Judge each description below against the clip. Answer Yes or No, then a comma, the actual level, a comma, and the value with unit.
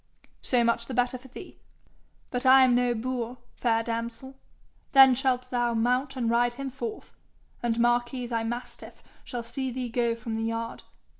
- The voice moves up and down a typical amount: No, narrow, 1.7 semitones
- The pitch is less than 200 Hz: No, high, 245 Hz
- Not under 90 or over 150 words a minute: No, average, 170 wpm